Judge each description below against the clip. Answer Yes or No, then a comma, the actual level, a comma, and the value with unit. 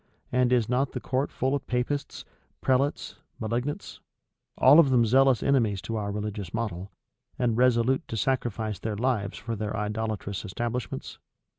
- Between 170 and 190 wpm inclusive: No, average, 150 wpm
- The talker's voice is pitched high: No, low, 115 Hz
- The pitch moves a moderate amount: Yes, average, 3.4 semitones